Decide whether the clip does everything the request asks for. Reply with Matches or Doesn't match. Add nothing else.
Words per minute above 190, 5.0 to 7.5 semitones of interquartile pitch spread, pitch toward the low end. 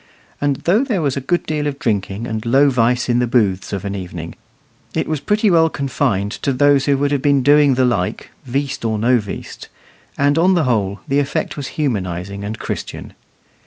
Matches